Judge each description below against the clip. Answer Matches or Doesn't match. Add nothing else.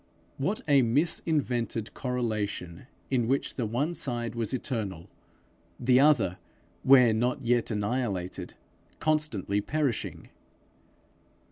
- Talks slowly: Matches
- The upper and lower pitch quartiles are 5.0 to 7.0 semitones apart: Doesn't match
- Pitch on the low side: Matches